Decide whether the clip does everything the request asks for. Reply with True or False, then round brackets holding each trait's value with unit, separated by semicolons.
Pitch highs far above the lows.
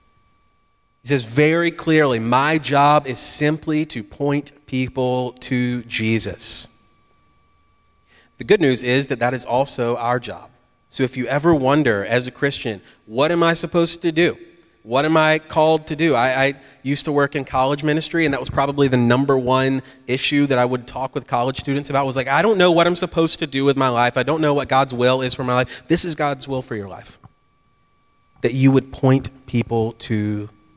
False (3.4 semitones)